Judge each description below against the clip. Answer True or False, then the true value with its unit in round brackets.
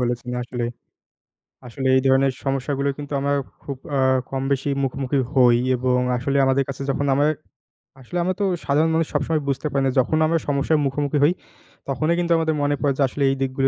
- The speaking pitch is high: False (140 Hz)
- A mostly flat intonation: True (1.8 semitones)